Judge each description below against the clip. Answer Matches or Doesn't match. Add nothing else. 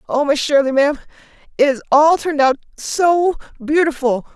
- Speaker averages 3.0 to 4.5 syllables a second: Doesn't match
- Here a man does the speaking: Doesn't match